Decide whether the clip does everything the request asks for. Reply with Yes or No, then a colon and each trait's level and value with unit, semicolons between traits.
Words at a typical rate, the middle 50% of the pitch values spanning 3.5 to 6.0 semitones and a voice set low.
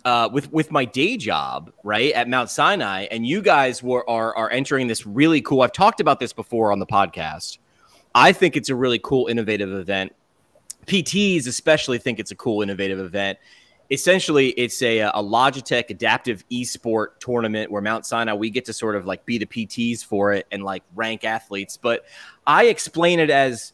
Yes: average, 190 wpm; average, 4.1 semitones; low, 115 Hz